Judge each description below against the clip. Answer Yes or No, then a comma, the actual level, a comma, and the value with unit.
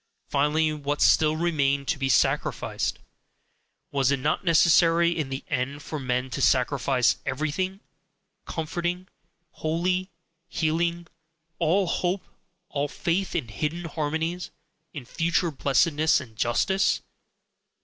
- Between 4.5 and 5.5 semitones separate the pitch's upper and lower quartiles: No, average, 3.4 semitones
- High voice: No, medium, 155 Hz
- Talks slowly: Yes, slow, 115 wpm